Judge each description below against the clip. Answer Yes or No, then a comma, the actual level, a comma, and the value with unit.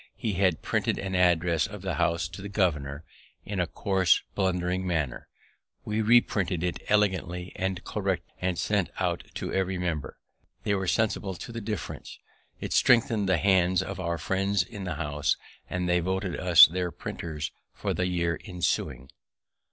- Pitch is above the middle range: No, very low, 90 Hz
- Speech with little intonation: Yes, narrow, 2.3 semitones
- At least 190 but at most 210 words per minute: No, average, 165 wpm